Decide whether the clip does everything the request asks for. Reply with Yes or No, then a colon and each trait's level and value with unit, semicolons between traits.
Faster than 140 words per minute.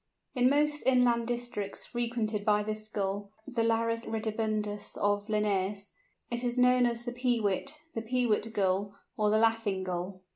Yes: average, 150 wpm